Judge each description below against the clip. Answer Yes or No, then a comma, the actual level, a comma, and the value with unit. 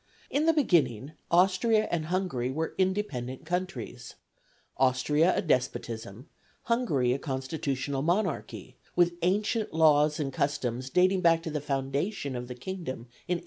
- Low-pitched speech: No, medium, 155 Hz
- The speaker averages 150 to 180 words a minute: No, average, 140 wpm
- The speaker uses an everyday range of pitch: No, wide, 5.8 semitones